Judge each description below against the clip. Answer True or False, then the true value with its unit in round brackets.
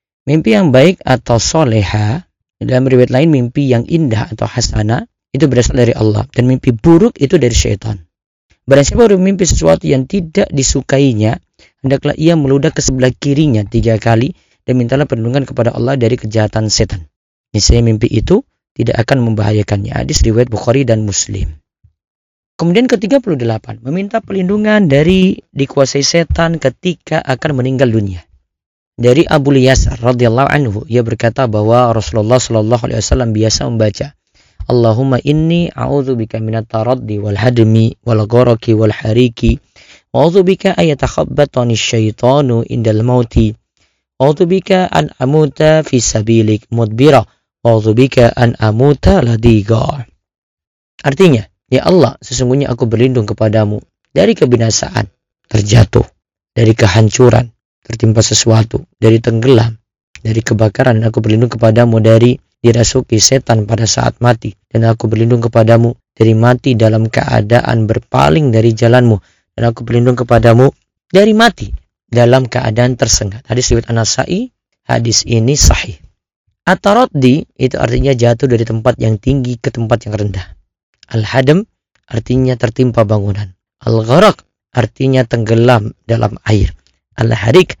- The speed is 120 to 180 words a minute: True (130 wpm)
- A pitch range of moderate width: True (3.4 semitones)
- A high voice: False (120 Hz)